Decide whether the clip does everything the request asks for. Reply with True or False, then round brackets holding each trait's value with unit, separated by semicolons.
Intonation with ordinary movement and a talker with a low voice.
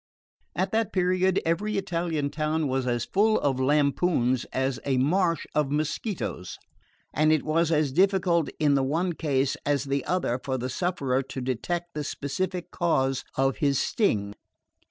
False (4.9 semitones; 150 Hz)